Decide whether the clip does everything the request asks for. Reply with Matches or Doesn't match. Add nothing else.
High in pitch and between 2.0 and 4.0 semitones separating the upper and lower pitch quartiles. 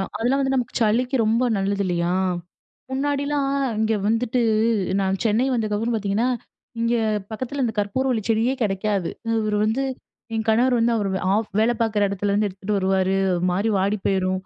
Matches